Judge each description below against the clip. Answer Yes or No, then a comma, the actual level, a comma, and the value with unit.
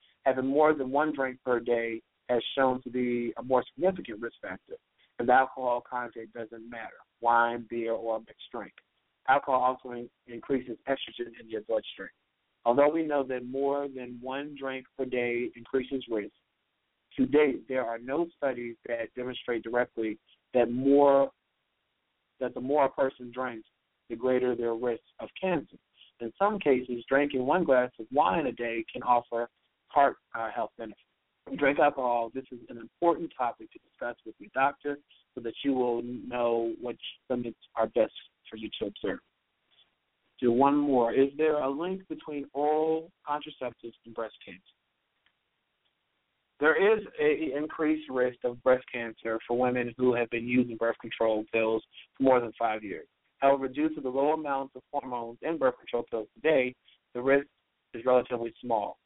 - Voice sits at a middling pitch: No, low, 125 Hz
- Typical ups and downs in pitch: Yes, average, 3.1 semitones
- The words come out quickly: No, average, 165 wpm